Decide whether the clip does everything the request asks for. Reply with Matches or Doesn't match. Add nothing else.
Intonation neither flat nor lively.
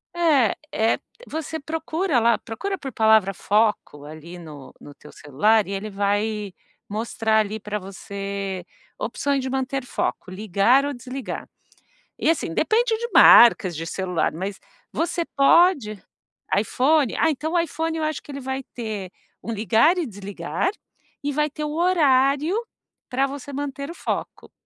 Doesn't match